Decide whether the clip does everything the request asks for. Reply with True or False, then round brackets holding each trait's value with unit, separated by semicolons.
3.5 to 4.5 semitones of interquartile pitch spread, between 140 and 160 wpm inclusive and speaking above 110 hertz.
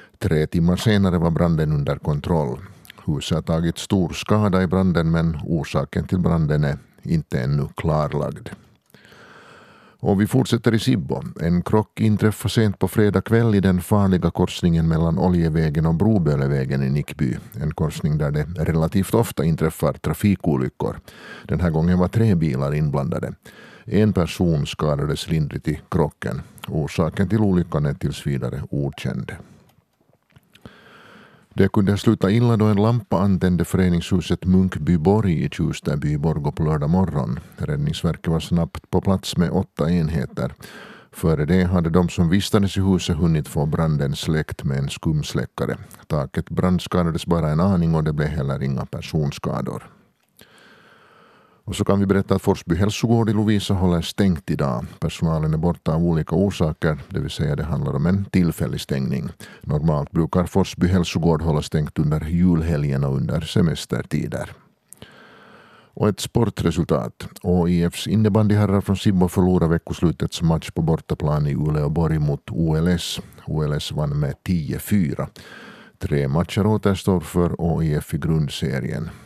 False (3.8 semitones; 145 wpm; 85 Hz)